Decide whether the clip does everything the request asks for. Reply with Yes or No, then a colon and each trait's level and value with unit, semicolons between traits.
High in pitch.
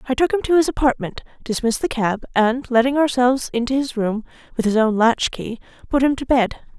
Yes: high, 245 Hz